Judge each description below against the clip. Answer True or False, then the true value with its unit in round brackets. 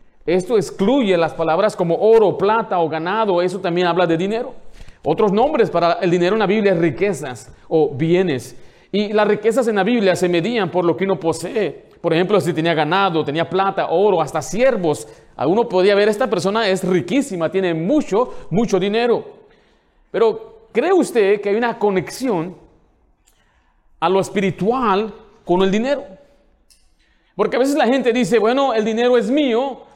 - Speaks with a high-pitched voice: True (200 Hz)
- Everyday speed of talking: True (170 wpm)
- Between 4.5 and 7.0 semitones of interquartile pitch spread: True (4.9 semitones)